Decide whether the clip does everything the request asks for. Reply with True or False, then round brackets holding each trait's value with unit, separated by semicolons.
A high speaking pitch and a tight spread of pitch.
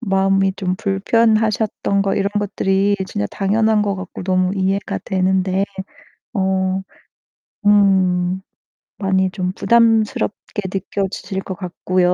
True (195 Hz; 1.5 semitones)